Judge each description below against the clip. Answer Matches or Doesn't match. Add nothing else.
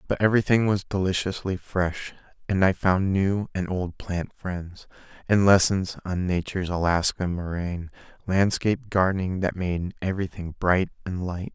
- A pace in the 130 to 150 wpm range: Matches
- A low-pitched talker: Matches